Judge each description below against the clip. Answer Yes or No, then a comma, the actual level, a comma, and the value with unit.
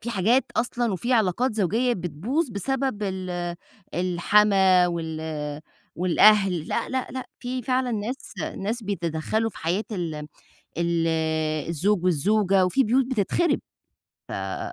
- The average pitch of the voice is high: Yes, high, 205 Hz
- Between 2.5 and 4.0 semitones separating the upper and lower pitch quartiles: No, wide, 5.4 semitones